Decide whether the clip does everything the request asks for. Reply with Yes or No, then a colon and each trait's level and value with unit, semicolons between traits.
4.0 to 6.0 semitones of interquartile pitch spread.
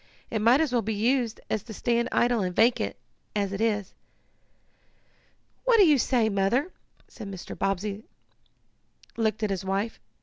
No: average, 3.4 semitones